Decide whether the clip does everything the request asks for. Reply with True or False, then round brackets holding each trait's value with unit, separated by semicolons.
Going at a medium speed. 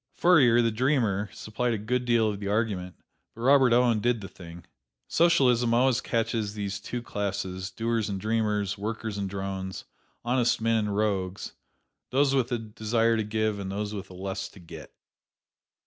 True (170 wpm)